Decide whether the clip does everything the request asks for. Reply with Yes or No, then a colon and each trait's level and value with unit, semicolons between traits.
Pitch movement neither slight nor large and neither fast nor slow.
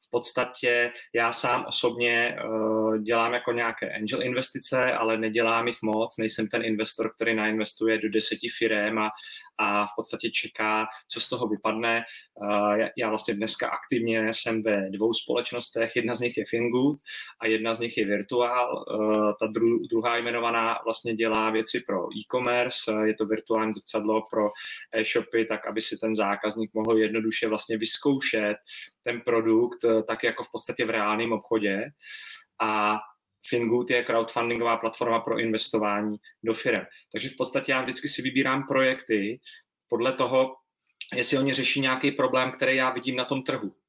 No: narrow, 1.6 semitones; average, 150 wpm